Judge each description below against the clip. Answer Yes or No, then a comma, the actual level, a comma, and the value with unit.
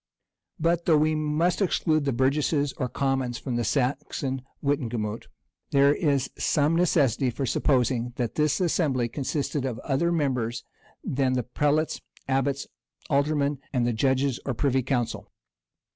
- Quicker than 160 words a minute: No, average, 140 wpm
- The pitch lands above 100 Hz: Yes, medium, 140 Hz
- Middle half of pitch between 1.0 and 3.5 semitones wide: Yes, average, 2.9 semitones